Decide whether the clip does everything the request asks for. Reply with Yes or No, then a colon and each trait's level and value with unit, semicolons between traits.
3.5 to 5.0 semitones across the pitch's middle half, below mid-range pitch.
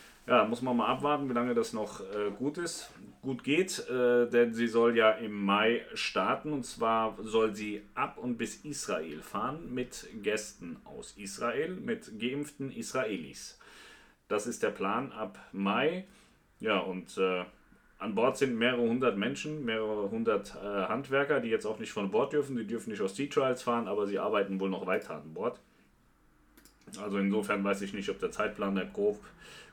Yes: average, 4.5 semitones; low, 115 Hz